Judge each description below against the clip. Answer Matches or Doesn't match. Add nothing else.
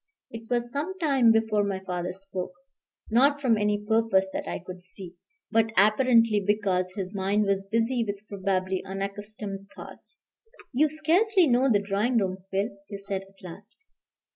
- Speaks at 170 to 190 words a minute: Doesn't match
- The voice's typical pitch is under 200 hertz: Doesn't match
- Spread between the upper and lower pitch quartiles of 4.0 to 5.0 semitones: Doesn't match